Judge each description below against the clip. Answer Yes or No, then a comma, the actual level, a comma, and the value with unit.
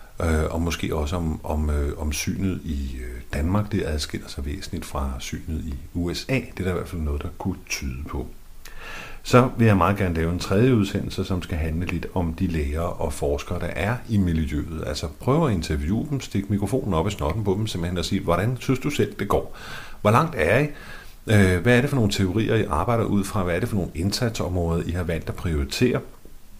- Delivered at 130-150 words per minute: No, average, 220 wpm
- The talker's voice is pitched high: No, very low, 90 Hz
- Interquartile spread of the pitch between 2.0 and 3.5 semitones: No, average, 4.4 semitones